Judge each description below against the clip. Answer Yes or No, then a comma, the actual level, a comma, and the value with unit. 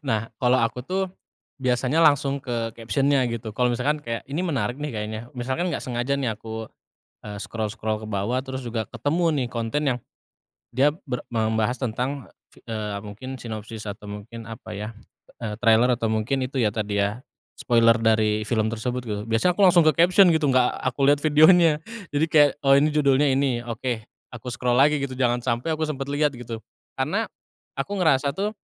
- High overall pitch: No, low, 125 Hz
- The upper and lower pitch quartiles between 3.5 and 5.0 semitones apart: Yes, average, 4.0 semitones